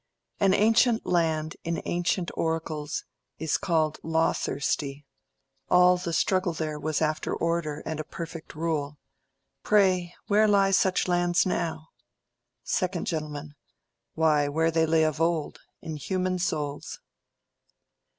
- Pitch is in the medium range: Yes, medium, 165 Hz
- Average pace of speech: No, slow, 120 wpm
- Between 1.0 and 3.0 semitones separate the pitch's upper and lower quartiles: Yes, narrow, 2.6 semitones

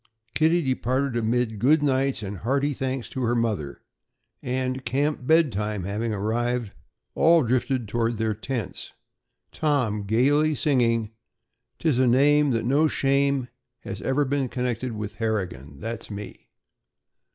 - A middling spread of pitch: Yes, average, 3.8 semitones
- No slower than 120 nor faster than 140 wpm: Yes, slow, 135 wpm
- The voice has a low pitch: Yes, low, 125 Hz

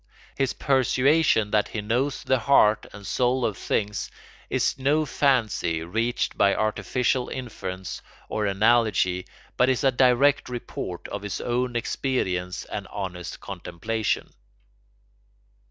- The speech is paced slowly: Yes, slow, 120 wpm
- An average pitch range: Yes, average, 4.5 semitones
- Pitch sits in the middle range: No, low, 115 Hz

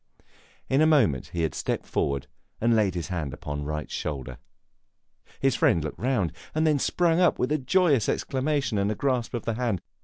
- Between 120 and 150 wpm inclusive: No, average, 185 wpm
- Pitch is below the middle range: Yes, low, 115 Hz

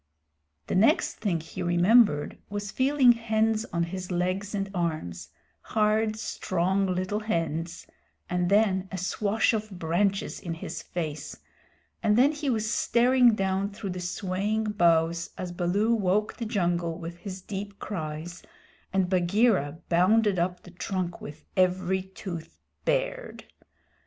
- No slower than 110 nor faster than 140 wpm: Yes, slow, 135 wpm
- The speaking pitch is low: No, high, 190 Hz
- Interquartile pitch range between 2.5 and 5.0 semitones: Yes, average, 3.6 semitones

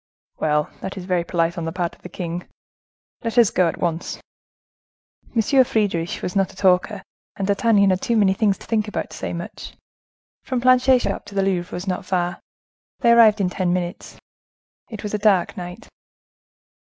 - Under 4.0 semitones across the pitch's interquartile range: Yes, average, 3.5 semitones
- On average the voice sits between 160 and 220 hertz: Yes, high, 190 Hz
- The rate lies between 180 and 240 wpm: Yes, average, 185 wpm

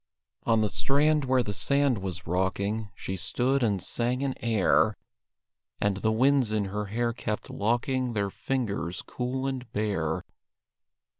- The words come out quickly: No, average, 145 wpm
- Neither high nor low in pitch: No, low, 115 Hz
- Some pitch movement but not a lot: Yes, average, 4.2 semitones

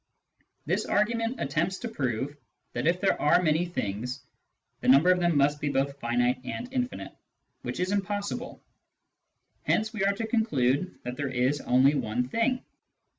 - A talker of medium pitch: Yes, medium, 155 Hz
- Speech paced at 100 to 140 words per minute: No, average, 170 wpm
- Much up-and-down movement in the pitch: Yes, wide, 7.6 semitones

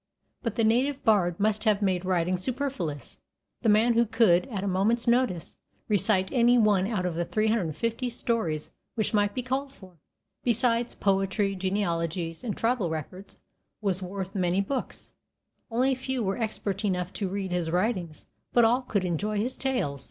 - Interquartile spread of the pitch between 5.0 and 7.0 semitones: No, average, 4.2 semitones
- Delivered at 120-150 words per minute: No, average, 165 wpm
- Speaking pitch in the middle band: No, high, 205 Hz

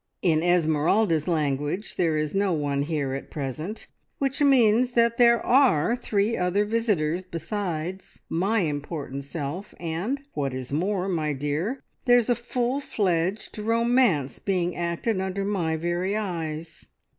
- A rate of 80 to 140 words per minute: Yes, slow, 135 wpm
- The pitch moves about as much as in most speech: No, wide, 5.9 semitones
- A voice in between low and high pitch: Yes, medium, 180 Hz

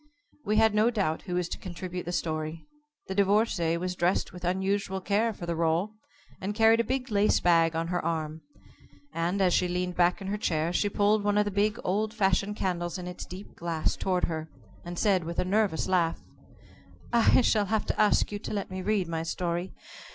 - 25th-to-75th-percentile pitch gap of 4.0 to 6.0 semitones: No, average, 3.3 semitones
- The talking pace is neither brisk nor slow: No, fast, 210 wpm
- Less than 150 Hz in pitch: No, medium, 185 Hz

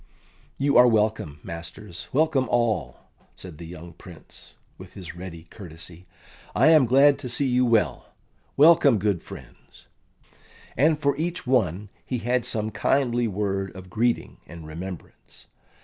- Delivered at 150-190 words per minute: No, average, 140 wpm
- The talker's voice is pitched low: Yes, low, 110 Hz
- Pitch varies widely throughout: Yes, wide, 6.4 semitones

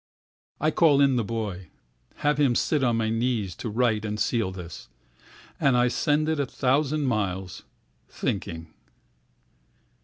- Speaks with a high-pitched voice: No, low, 115 Hz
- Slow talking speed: Yes, slow, 130 wpm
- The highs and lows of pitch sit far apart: Yes, wide, 6.3 semitones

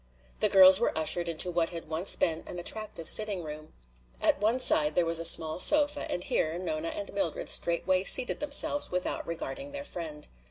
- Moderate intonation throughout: No, wide, 5.8 semitones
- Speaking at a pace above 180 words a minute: Yes, average, 190 wpm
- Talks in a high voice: No, medium, 180 Hz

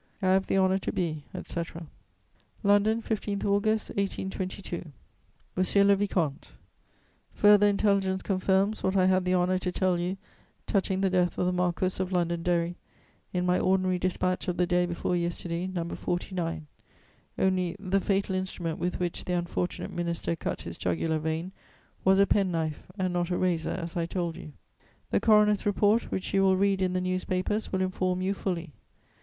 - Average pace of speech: Yes, average, 170 wpm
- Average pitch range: No, narrow, 1.8 semitones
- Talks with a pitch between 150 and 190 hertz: Yes, medium, 185 Hz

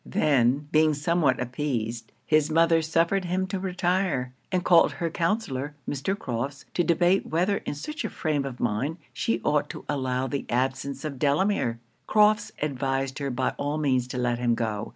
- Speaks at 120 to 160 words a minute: No, average, 175 wpm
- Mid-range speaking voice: Yes, medium, 145 Hz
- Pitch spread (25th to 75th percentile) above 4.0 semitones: Yes, average, 4.9 semitones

